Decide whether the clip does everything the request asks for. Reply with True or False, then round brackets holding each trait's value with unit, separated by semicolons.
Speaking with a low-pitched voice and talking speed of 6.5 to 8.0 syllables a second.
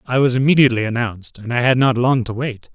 True (125 Hz; 6.6 syllables/s)